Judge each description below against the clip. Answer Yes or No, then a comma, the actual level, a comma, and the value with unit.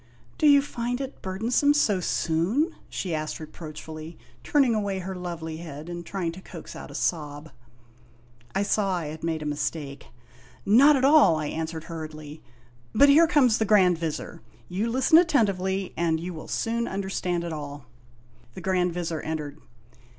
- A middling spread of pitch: No, wide, 5.9 semitones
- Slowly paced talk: No, average, 180 wpm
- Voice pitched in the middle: Yes, medium, 180 Hz